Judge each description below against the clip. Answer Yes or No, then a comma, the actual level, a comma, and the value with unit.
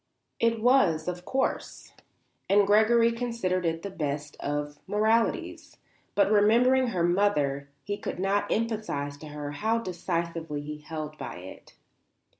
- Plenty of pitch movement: Yes, wide, 6.6 semitones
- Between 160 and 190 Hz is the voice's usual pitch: Yes, medium, 185 Hz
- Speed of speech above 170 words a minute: No, average, 140 wpm